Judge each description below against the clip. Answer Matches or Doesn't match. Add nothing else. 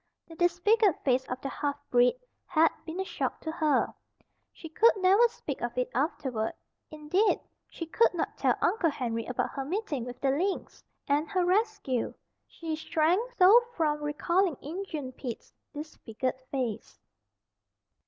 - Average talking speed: Matches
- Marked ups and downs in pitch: Matches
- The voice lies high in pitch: Matches